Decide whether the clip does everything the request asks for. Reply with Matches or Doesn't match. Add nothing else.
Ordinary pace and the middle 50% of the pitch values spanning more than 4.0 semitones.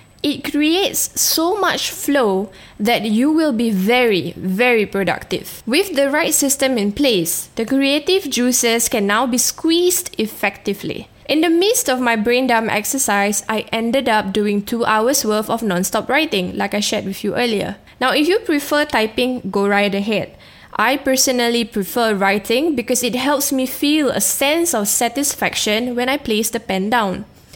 Matches